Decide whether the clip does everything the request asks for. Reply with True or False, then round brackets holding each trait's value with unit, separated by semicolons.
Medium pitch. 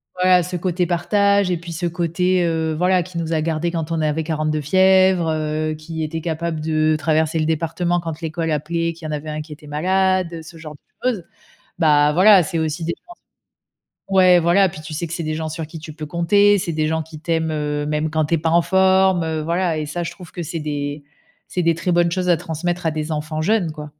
True (165 Hz)